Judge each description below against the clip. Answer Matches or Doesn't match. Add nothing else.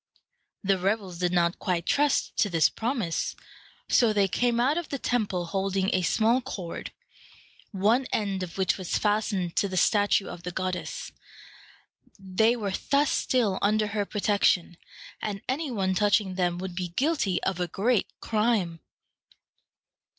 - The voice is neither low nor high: Doesn't match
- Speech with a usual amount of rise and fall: Matches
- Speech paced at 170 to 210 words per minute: Doesn't match